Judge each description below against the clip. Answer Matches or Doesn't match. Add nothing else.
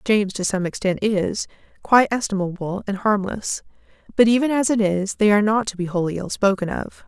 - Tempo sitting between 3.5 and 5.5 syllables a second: Doesn't match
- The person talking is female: Matches